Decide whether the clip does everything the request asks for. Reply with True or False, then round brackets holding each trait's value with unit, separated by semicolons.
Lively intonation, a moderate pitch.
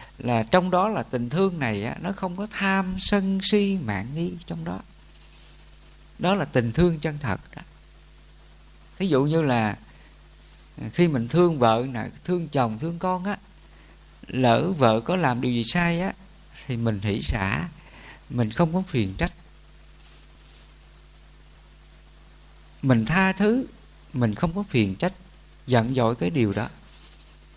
True (7.6 semitones; 160 Hz)